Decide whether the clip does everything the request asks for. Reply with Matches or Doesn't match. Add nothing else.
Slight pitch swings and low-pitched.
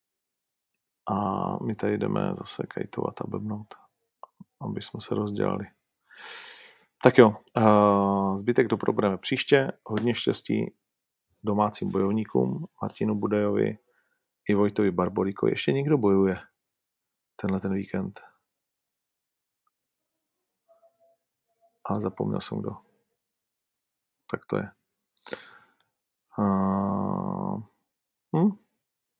Doesn't match